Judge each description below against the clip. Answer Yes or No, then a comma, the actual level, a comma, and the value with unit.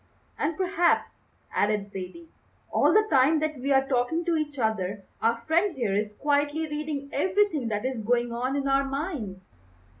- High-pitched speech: Yes, very high, 275 Hz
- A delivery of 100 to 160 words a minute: No, average, 170 wpm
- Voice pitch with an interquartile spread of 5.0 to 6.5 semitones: Yes, wide, 5.5 semitones